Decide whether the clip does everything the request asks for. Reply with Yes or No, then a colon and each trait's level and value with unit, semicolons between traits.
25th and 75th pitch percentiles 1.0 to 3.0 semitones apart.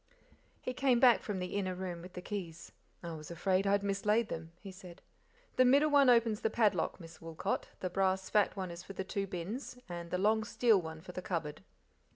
No: average, 3.8 semitones